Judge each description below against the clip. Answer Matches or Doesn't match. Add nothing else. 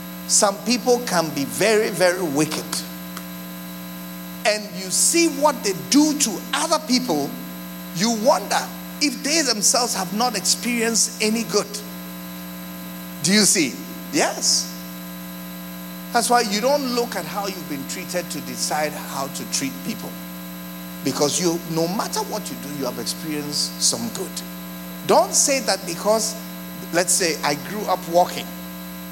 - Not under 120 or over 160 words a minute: Matches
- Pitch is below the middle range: Doesn't match